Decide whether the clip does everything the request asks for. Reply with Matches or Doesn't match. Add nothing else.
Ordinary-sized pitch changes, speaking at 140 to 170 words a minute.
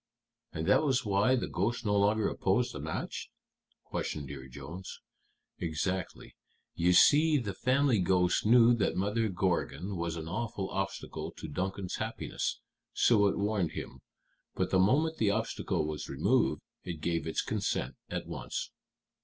Matches